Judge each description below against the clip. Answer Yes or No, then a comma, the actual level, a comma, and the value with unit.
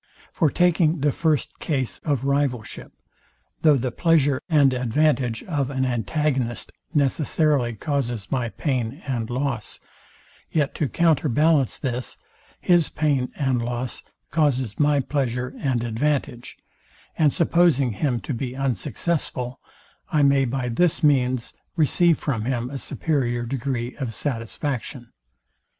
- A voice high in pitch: No, low, 135 Hz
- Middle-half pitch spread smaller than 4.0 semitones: Yes, average, 3.5 semitones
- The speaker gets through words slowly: Yes, slow, 125 wpm